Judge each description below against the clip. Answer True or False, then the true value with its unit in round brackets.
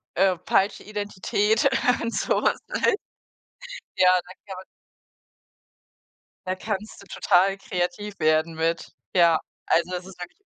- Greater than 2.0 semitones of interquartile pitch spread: True (2.4 semitones)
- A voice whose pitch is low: False (185 Hz)